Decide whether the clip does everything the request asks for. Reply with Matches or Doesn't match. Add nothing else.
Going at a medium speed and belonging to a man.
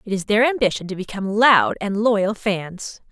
Doesn't match